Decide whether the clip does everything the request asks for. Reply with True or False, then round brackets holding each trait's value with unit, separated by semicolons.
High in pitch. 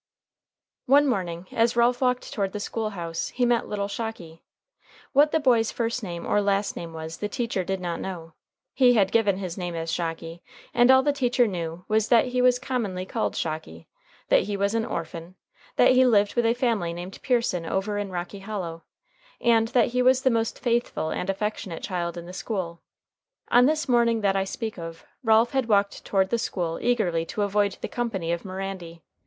True (205 Hz)